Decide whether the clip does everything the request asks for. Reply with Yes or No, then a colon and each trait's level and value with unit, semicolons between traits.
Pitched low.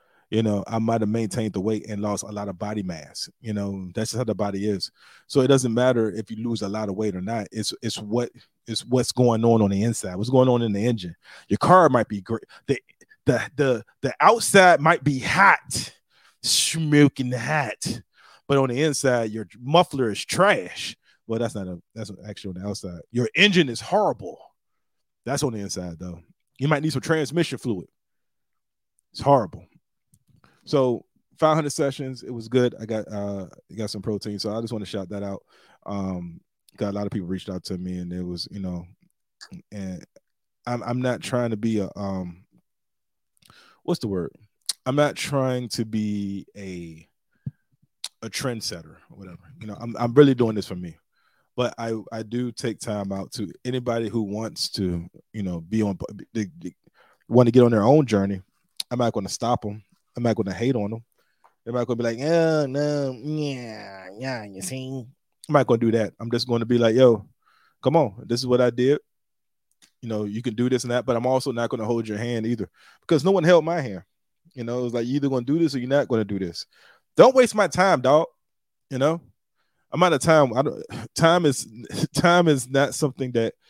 Yes: low, 115 Hz